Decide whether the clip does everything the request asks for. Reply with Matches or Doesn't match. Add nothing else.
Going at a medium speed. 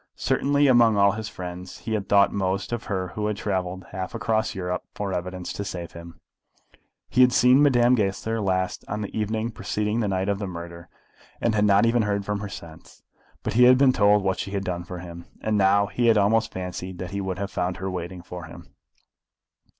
Doesn't match